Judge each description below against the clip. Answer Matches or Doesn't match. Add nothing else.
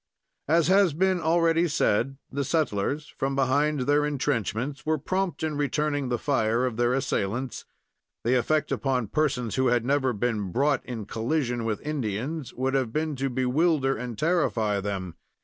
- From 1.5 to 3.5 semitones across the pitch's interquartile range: Doesn't match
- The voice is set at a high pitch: Doesn't match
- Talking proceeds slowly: Doesn't match